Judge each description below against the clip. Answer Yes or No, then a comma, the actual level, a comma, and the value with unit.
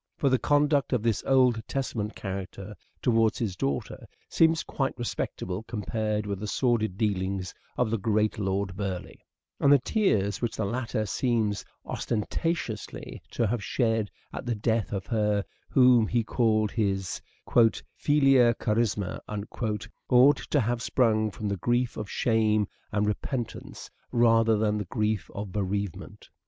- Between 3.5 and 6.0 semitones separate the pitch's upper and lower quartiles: No, average, 2.8 semitones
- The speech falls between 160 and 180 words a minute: No, average, 150 wpm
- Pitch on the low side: Yes, low, 110 Hz